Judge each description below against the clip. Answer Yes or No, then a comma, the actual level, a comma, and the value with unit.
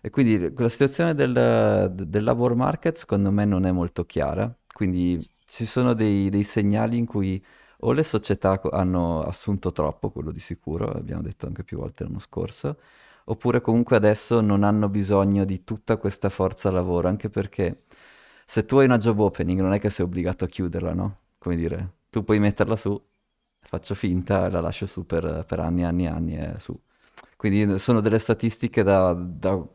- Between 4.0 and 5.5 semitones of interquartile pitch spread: No, average, 3.6 semitones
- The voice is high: No, low, 100 Hz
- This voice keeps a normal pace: No, fast, 185 wpm